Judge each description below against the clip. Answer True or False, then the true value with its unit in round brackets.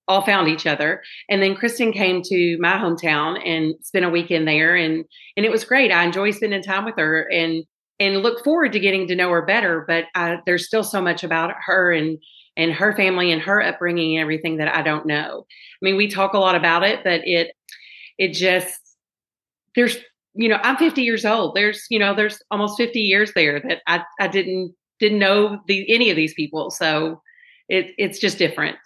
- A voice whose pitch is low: False (185 Hz)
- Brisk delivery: True (210 wpm)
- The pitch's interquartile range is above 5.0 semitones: False (3.9 semitones)